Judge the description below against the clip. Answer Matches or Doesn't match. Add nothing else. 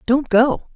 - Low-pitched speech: Doesn't match